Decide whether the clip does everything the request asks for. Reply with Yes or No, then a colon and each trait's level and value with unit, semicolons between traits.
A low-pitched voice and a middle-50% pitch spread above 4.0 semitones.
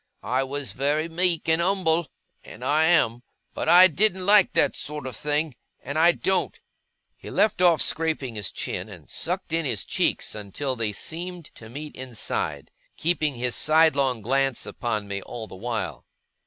No: medium, 150 Hz; wide, 5.5 semitones